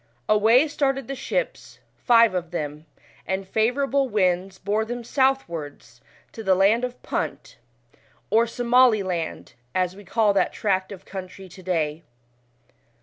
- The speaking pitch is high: Yes, high, 205 Hz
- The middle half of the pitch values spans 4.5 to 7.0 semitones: Yes, average, 4.8 semitones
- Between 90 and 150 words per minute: Yes, average, 140 wpm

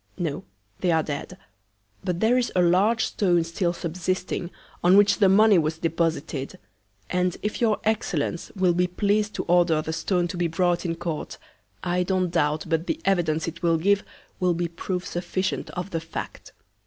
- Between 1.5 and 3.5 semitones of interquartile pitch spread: Yes, narrow, 2.4 semitones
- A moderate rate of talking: Yes, average, 180 wpm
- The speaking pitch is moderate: Yes, medium, 175 Hz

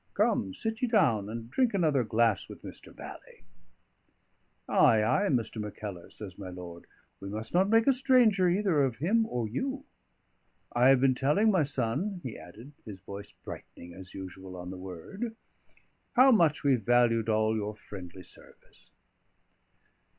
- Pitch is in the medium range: No, low, 120 Hz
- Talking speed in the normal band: Yes, average, 160 wpm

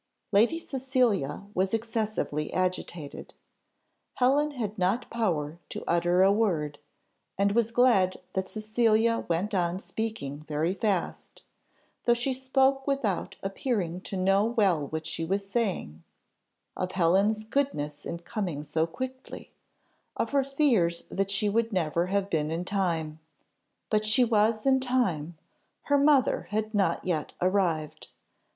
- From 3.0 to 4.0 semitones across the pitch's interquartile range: No, average, 5.3 semitones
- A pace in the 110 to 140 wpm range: Yes, slow, 135 wpm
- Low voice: No, high, 200 Hz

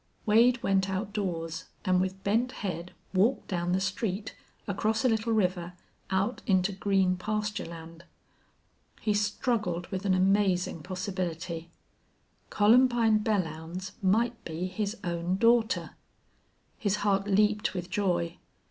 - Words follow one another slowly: Yes, slow, 120 wpm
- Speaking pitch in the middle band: No, high, 195 Hz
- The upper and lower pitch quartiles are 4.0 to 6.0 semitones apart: No, average, 2.9 semitones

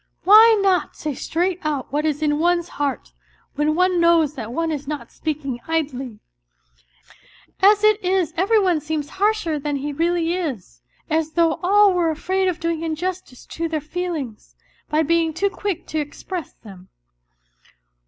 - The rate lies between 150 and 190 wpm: Yes, average, 160 wpm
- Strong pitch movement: No, average, 3.4 semitones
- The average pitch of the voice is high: Yes, very high, 325 Hz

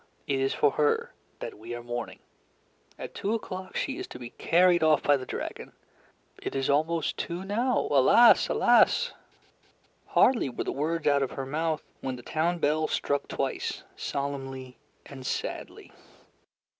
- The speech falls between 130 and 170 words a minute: Yes, average, 155 wpm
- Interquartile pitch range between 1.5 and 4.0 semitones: No, average, 4.4 semitones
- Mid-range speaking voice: Yes, medium, 150 Hz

